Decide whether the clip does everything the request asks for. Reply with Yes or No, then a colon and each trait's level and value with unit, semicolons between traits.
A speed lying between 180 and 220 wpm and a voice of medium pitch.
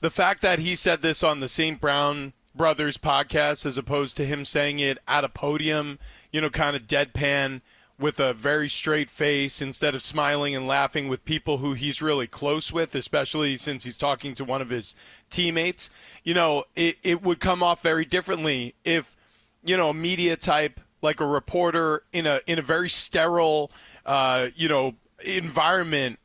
Yes: average, 185 wpm; medium, 150 Hz